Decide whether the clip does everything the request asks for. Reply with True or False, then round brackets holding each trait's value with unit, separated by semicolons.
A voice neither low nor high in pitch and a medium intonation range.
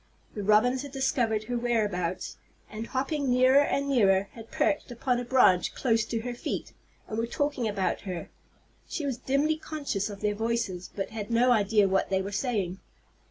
False (230 Hz; 4.3 semitones)